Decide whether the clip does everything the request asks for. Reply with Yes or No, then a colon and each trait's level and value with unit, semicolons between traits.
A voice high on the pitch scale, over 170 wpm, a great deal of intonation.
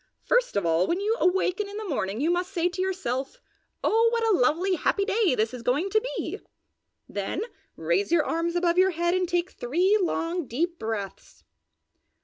Yes: very high, 350 Hz; average, 185 wpm; wide, 5.9 semitones